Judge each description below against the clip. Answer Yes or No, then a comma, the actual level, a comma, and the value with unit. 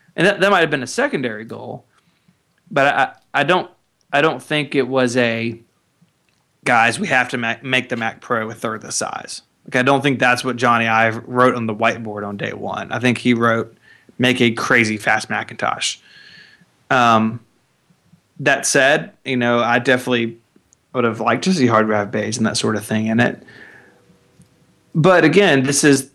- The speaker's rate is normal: Yes, average, 195 wpm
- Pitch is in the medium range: No, low, 120 Hz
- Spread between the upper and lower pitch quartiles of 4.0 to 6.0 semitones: No, narrow, 2.4 semitones